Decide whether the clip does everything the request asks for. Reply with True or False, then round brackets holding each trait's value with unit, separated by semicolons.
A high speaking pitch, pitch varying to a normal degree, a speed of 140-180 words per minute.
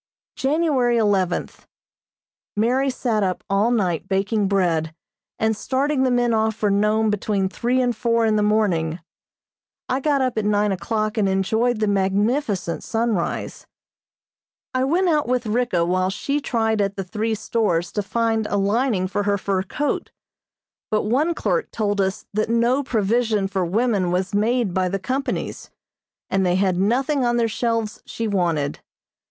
True (215 Hz; 3.8 semitones; 160 wpm)